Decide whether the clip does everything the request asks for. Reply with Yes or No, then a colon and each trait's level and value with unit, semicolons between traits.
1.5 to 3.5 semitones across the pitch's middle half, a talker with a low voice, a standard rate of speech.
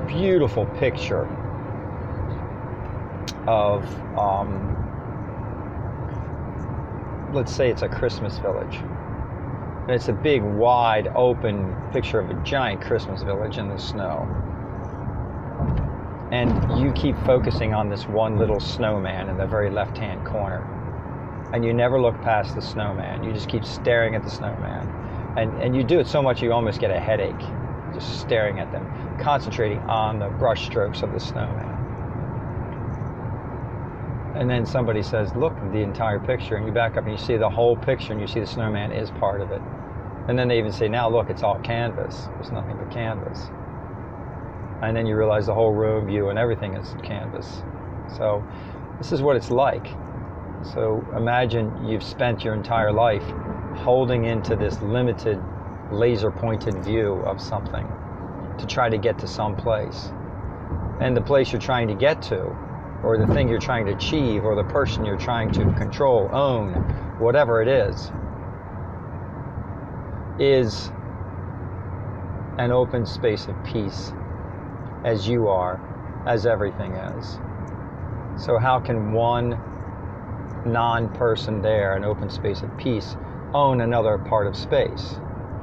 Yes: average, 3.0 semitones; low, 110 Hz; average, 150 wpm